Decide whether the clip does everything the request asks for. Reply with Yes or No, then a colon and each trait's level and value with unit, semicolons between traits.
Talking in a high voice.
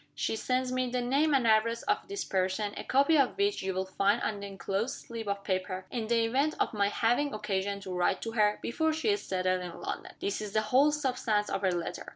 Yes: high, 220 Hz